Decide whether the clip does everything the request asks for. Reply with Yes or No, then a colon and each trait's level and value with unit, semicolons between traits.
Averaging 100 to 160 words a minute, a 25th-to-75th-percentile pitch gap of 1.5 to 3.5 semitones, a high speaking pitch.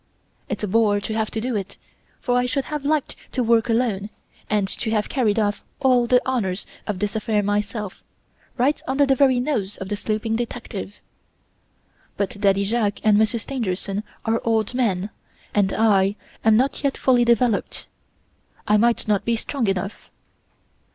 No: average, 170 wpm; average, 3.2 semitones; high, 220 Hz